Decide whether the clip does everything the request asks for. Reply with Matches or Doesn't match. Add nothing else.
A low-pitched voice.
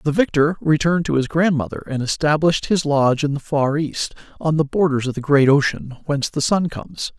Doesn't match